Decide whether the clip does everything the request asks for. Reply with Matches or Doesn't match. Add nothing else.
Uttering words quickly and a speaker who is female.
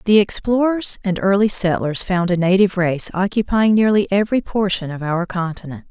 Doesn't match